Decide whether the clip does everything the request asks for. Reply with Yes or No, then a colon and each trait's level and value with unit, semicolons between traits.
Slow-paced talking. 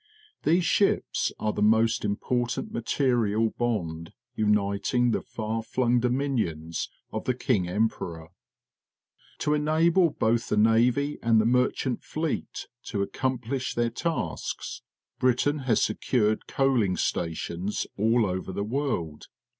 Yes: slow, 125 wpm